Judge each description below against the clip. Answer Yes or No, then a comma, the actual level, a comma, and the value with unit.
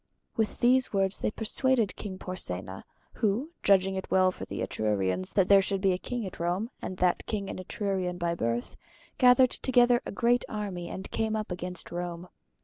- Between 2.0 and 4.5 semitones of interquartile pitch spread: Yes, average, 3.7 semitones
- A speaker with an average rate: Yes, average, 185 wpm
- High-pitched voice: Yes, high, 195 Hz